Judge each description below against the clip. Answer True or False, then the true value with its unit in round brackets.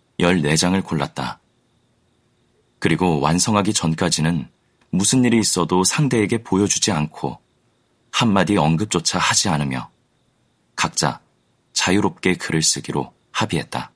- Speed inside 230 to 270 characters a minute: True (260 characters per minute)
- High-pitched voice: False (90 Hz)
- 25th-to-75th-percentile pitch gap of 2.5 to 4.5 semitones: False (5.1 semitones)